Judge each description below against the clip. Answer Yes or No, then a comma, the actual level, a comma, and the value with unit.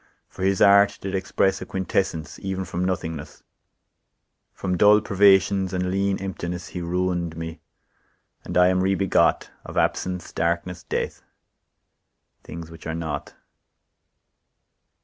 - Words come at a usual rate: No, slow, 125 wpm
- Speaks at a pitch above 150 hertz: No, very low, 90 Hz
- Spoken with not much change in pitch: Yes, narrow, 2.2 semitones